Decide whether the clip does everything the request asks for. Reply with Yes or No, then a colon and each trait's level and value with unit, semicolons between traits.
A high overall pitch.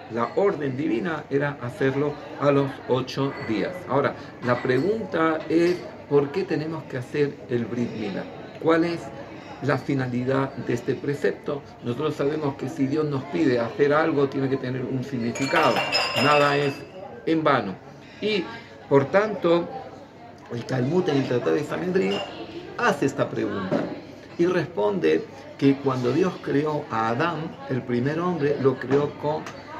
No: medium, 140 Hz